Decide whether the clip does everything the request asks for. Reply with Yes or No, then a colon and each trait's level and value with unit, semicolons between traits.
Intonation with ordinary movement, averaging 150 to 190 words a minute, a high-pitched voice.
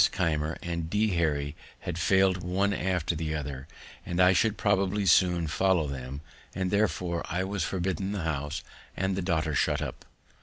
No: average, 3.3 semitones; average, 165 wpm; very low, 90 Hz